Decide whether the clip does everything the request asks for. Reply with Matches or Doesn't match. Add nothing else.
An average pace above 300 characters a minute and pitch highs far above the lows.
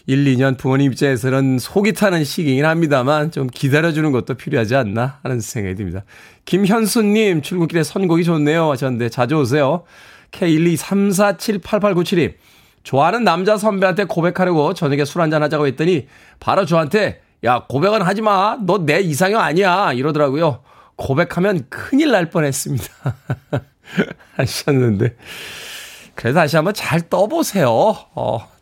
Matches